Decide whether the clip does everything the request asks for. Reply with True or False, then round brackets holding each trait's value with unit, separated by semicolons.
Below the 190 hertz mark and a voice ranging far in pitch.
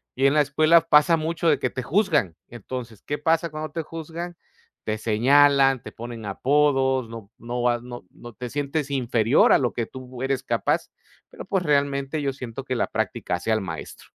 False (135 Hz; 3.8 semitones)